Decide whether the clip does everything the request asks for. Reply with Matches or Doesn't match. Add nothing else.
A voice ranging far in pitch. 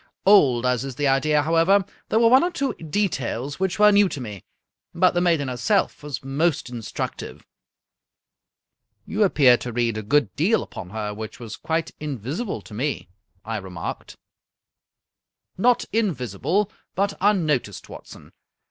Matches